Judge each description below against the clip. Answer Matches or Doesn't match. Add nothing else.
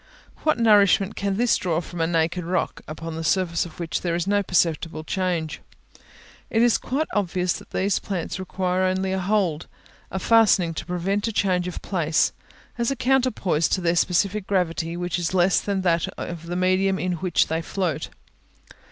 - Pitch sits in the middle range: Matches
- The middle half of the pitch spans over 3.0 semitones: Doesn't match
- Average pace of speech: Matches